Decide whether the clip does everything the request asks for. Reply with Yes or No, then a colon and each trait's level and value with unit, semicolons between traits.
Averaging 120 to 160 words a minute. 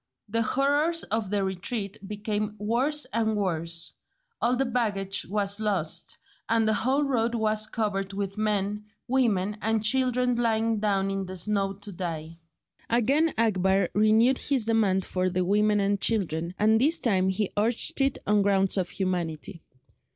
Yes: average, 155 wpm